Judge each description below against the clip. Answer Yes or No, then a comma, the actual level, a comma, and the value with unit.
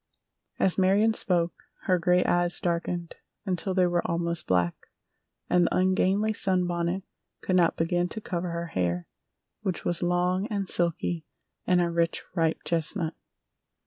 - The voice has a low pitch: No, medium, 175 Hz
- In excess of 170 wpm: No, average, 145 wpm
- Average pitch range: No, narrow, 1.6 semitones